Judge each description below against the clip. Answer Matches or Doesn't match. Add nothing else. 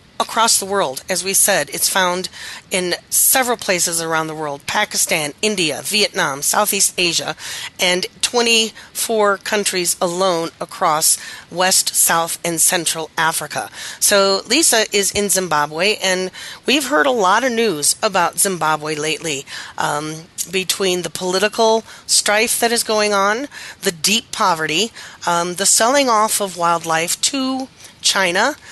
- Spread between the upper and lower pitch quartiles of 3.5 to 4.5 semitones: Matches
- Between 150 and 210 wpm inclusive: Doesn't match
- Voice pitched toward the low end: Doesn't match